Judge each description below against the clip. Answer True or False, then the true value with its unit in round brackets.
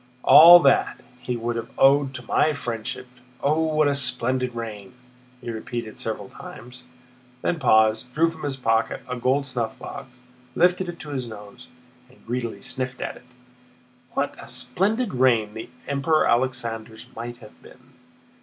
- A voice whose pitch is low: True (125 Hz)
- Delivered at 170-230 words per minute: False (155 wpm)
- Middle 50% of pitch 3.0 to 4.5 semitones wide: True (3.4 semitones)